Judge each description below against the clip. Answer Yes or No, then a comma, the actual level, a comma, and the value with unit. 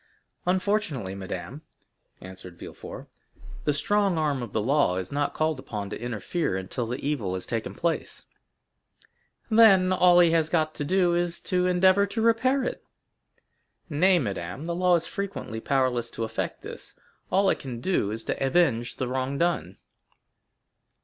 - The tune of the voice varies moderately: No, wide, 7.8 semitones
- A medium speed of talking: Yes, average, 155 wpm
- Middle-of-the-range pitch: Yes, medium, 150 Hz